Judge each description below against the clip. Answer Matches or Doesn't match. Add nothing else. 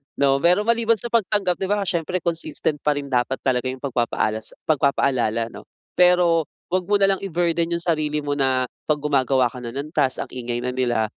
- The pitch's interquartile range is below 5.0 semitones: Doesn't match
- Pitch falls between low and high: Matches